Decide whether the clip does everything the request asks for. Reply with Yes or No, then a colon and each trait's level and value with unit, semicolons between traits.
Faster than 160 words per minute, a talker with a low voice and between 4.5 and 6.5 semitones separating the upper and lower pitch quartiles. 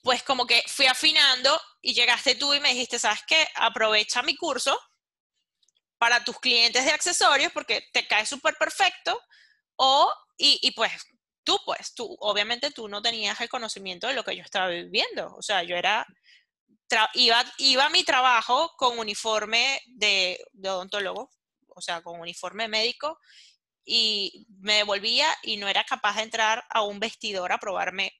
No: average, 170 wpm; high, 240 Hz; average, 5.1 semitones